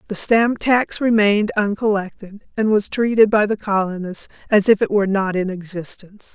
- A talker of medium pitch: No, high, 205 Hz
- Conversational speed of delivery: Yes, average, 170 wpm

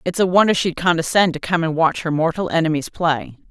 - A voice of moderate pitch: Yes, medium, 165 Hz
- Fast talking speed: Yes, fast, 220 wpm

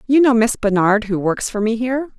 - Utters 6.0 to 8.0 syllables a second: No, 5.6 syllables/s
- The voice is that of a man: No, female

